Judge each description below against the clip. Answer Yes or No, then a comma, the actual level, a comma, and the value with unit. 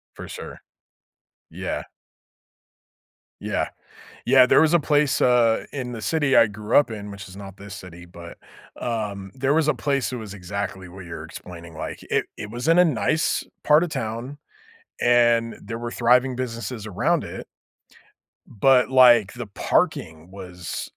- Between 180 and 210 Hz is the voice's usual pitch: No, low, 115 Hz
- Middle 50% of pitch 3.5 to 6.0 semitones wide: Yes, average, 4.7 semitones